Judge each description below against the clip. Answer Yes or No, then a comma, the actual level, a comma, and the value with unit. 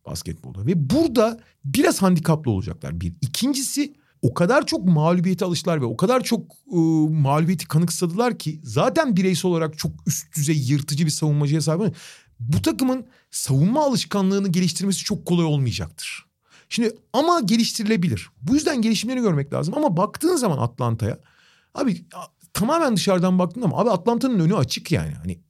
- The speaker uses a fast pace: Yes, fast, 145 wpm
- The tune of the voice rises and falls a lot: Yes, wide, 7.1 semitones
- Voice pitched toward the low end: No, medium, 175 Hz